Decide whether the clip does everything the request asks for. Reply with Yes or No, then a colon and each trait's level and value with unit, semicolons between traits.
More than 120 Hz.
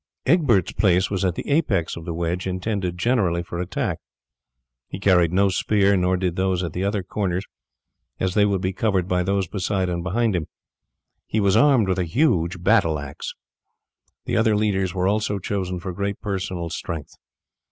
No: very low, 95 Hz